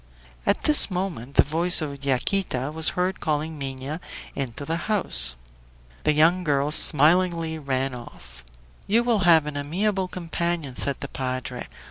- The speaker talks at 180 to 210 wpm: No, average, 145 wpm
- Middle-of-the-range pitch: Yes, medium, 155 Hz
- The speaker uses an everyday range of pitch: Yes, average, 4.6 semitones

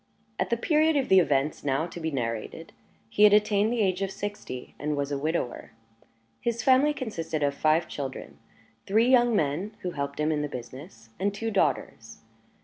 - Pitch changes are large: Yes, wide, 6.9 semitones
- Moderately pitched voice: Yes, medium, 175 Hz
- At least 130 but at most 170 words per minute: No, average, 185 wpm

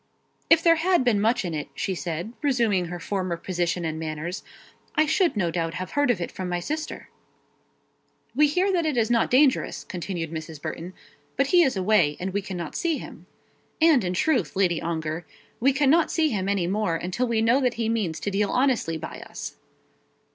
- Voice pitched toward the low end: No, high, 200 Hz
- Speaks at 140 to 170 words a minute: No, average, 200 wpm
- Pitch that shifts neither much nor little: No, wide, 7.6 semitones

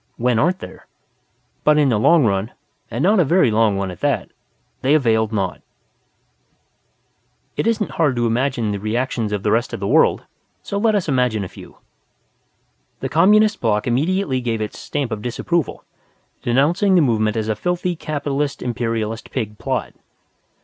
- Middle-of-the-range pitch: No, low, 125 Hz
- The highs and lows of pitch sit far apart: Yes, wide, 6.3 semitones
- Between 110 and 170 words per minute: Yes, average, 165 wpm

